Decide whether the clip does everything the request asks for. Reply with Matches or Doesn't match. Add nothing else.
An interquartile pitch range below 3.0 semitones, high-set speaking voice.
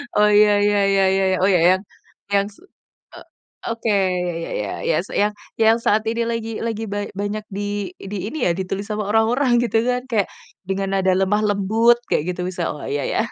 Matches